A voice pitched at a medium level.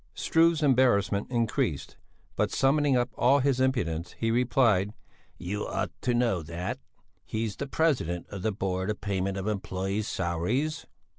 No: low, 110 Hz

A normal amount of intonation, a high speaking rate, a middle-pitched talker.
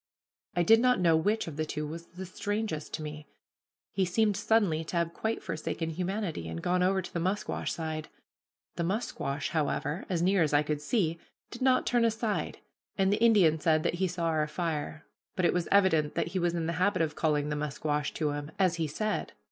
Yes: average, 4.0 semitones; fast, 210 wpm; medium, 170 Hz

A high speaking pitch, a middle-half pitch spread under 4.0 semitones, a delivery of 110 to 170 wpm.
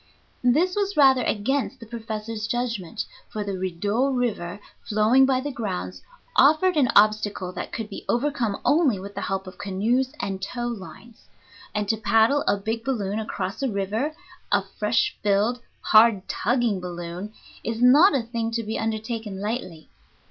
Yes: high, 220 Hz; average, 3.6 semitones; average, 160 wpm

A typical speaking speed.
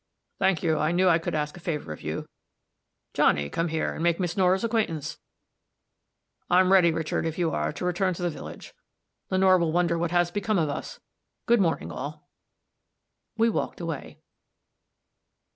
Yes: average, 170 wpm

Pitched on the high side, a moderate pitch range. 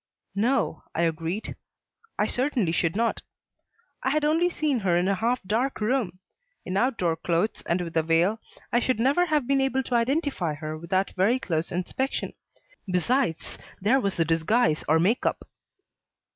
No: high, 210 Hz; wide, 7.4 semitones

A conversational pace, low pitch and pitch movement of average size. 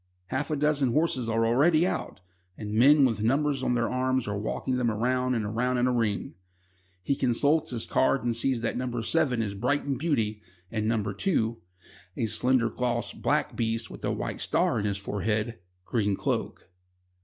Yes: average, 180 wpm; low, 120 Hz; average, 3.0 semitones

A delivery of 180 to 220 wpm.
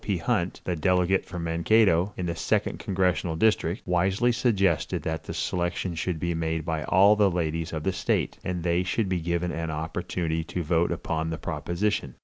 Yes: average, 185 wpm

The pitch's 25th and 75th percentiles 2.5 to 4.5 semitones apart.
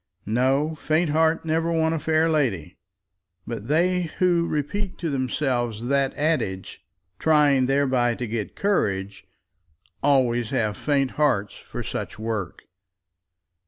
No: average, 5.3 semitones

